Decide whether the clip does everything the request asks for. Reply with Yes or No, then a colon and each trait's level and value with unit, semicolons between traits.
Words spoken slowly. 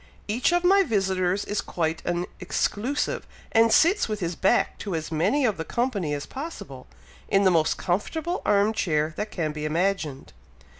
No: average, 170 wpm